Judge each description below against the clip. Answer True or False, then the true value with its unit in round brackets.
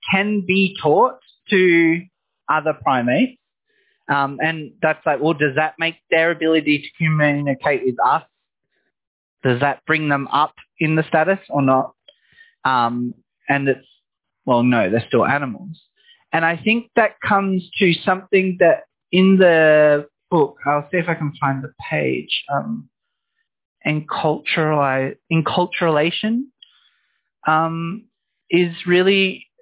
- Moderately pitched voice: True (165 Hz)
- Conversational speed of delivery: False (130 wpm)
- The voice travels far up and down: False (4.6 semitones)